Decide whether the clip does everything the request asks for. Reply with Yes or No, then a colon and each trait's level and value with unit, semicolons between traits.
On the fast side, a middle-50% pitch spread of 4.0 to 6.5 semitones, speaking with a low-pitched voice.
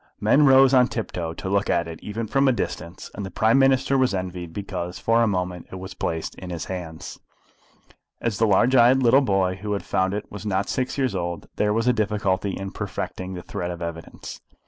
Yes: fast, 225 wpm; average, 4.5 semitones; low, 100 Hz